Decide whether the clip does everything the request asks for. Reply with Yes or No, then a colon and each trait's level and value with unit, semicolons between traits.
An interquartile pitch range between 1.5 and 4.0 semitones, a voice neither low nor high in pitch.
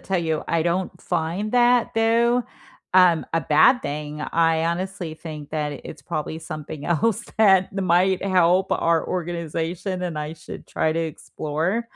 Yes: average, 3.2 semitones; medium, 170 Hz